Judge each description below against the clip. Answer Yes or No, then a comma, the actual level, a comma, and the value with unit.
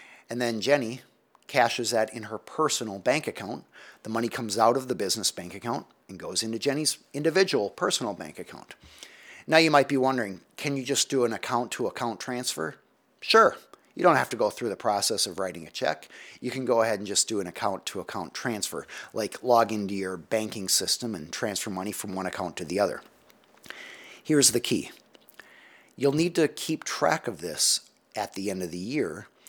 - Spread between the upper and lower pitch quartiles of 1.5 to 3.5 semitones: No, average, 5.1 semitones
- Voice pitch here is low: Yes, low, 120 Hz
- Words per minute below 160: No, average, 195 wpm